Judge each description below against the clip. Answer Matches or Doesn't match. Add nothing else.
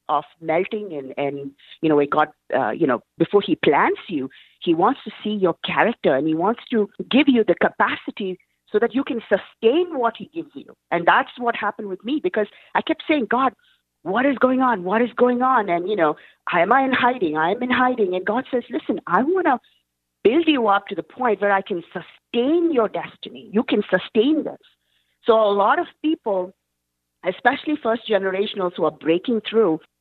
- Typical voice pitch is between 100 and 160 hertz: Doesn't match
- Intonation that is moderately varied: Doesn't match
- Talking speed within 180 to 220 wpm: Matches